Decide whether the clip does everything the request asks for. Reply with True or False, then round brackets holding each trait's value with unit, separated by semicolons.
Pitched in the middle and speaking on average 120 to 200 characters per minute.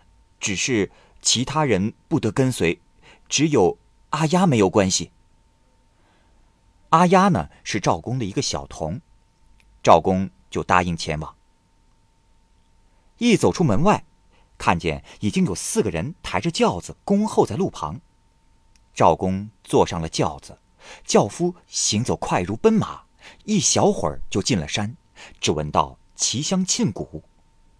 False (100 Hz; 190 characters per minute)